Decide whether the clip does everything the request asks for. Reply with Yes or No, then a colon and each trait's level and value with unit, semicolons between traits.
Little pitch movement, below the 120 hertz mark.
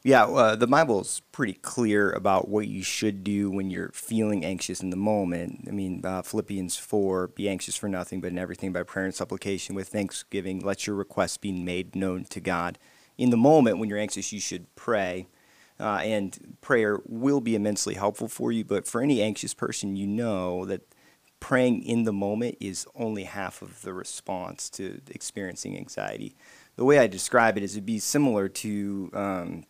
Yes: narrow, 2.2 semitones; low, 100 Hz